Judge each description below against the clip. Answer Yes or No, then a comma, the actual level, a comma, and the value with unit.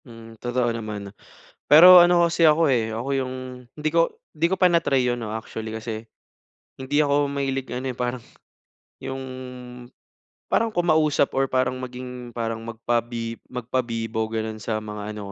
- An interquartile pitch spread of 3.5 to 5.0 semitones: Yes, average, 4.3 semitones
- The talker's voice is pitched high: No, low, 125 Hz